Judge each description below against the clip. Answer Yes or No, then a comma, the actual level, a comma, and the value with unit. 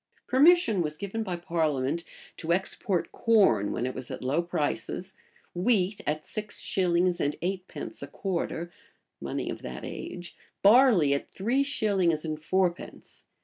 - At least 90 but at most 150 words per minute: Yes, average, 145 wpm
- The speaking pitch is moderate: Yes, medium, 180 Hz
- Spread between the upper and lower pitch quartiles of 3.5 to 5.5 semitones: Yes, average, 4.6 semitones